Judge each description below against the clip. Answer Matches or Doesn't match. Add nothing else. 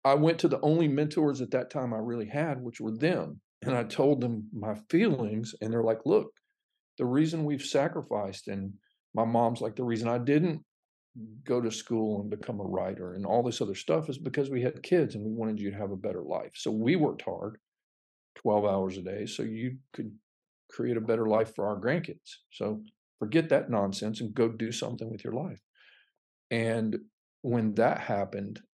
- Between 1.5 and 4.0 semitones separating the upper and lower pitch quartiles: Doesn't match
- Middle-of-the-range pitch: Doesn't match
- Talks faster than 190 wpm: Matches